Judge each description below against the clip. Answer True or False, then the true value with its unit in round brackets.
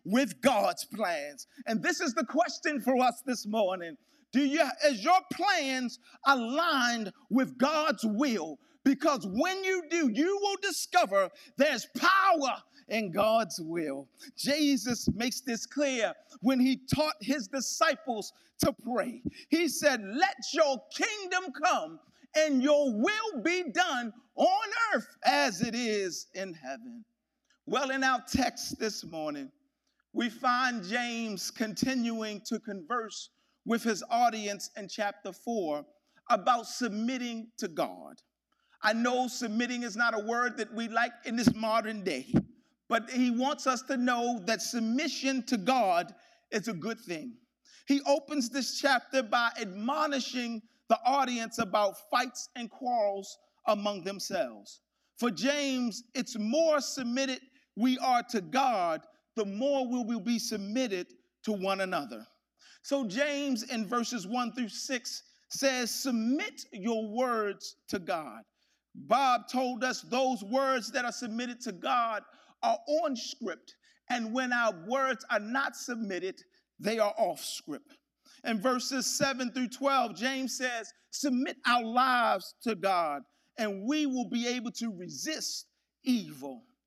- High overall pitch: True (250 Hz)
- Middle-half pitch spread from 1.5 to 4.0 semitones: True (3.7 semitones)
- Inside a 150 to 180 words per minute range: False (140 wpm)